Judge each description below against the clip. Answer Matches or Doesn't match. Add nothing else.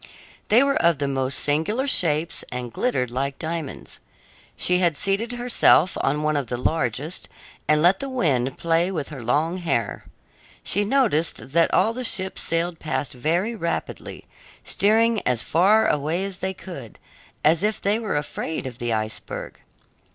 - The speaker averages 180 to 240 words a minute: Doesn't match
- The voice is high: Doesn't match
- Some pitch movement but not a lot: Doesn't match